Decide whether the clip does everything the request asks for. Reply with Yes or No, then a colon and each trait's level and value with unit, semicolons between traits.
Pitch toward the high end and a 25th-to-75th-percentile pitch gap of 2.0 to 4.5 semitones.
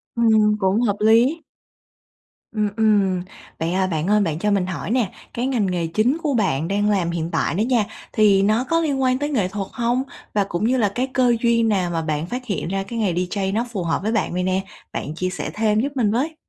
Yes: high, 210 Hz; average, 4.2 semitones